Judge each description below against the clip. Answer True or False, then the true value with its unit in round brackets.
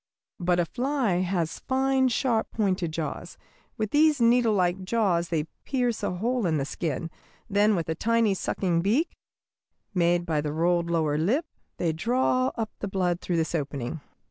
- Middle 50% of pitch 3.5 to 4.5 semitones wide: False (5.6 semitones)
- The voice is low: False (185 Hz)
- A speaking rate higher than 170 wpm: False (165 wpm)